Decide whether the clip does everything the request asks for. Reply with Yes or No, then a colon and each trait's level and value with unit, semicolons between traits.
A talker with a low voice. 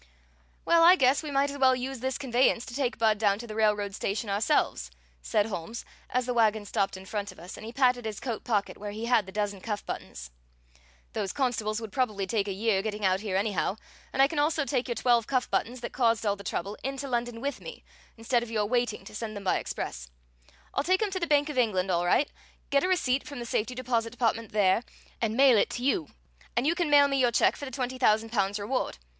No: high, 230 Hz